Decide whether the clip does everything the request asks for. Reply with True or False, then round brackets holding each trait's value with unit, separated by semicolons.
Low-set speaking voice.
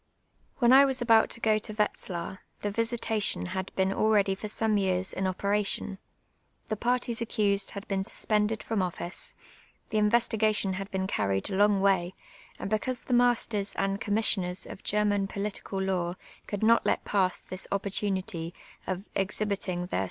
False (200 Hz)